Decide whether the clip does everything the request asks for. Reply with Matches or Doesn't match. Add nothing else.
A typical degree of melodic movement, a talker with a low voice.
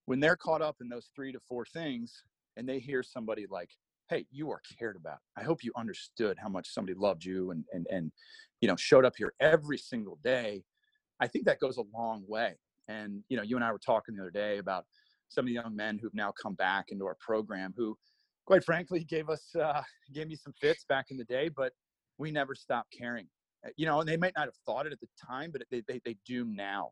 Doesn't match